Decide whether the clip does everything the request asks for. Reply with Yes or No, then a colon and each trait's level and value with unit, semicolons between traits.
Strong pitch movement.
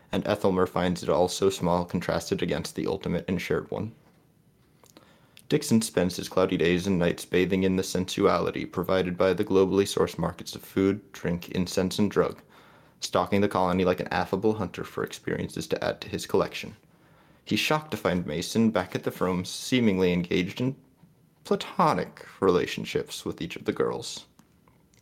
No: average, 2.8 semitones